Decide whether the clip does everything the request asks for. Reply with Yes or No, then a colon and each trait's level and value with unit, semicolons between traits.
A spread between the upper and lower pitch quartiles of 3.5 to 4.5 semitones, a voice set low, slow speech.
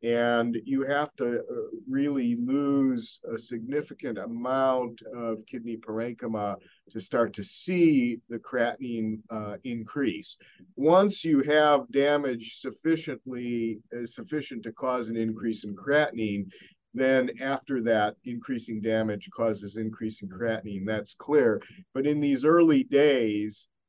Yes: average, 4.2 semitones; low, 120 Hz; slow, 125 wpm